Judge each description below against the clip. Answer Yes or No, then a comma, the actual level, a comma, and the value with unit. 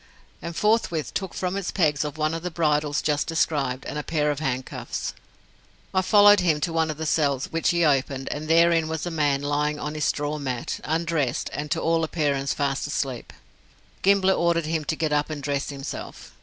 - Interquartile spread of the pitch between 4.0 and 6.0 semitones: No, narrow, 2.4 semitones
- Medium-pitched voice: Yes, medium, 155 Hz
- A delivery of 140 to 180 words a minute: No, average, 195 wpm